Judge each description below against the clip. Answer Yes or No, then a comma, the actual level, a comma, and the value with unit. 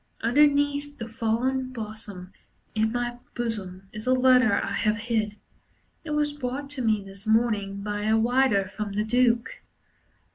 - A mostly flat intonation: No, average, 3.5 semitones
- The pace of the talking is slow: No, average, 150 wpm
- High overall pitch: Yes, high, 230 Hz